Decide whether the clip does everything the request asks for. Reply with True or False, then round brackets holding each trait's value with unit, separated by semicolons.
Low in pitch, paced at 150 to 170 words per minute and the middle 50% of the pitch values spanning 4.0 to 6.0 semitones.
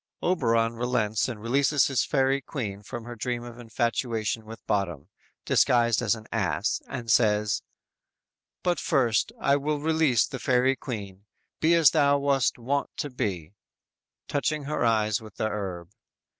True (120 Hz; 155 wpm; 4.3 semitones)